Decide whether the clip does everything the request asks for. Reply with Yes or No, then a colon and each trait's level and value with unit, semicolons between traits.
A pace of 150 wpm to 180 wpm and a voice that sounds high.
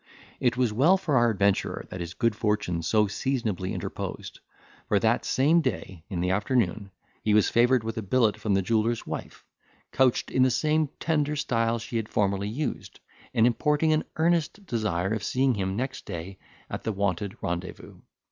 No: average, 175 wpm; low, 115 Hz